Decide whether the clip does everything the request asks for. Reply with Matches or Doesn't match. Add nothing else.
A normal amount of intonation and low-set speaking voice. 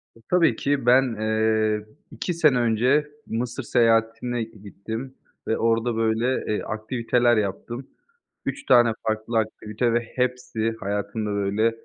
Doesn't match